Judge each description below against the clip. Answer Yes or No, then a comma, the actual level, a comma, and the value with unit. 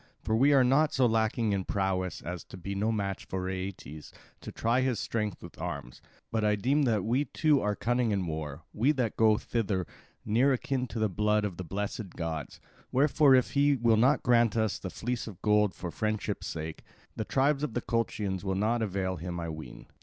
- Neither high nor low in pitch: No, low, 105 Hz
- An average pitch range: Yes, average, 4.4 semitones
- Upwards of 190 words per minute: Yes, fast, 205 wpm